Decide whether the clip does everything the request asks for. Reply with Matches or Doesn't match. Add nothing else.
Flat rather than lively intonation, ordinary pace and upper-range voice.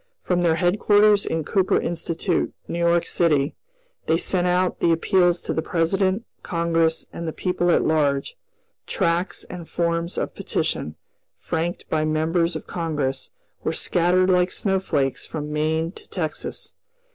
Doesn't match